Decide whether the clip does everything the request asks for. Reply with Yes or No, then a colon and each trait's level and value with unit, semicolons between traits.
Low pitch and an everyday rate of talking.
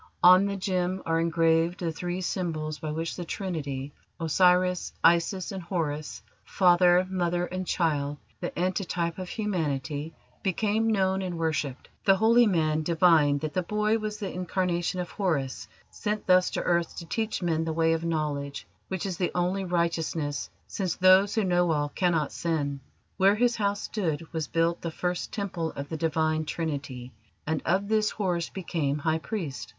No: medium, 175 Hz; average, 165 wpm